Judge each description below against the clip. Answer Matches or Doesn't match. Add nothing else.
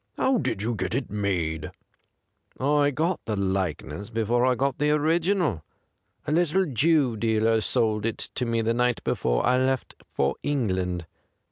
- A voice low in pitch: Matches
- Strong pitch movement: Matches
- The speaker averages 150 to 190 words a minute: Matches